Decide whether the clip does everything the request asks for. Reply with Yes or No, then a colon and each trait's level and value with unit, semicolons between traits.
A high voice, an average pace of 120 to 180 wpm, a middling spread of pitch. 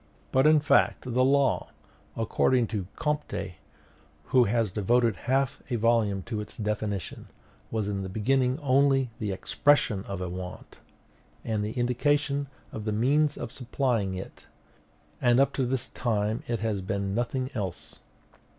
No: low, 115 Hz; average, 155 wpm; average, 4.3 semitones